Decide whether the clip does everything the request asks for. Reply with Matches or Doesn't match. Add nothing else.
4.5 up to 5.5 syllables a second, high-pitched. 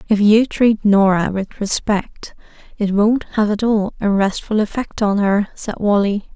Doesn't match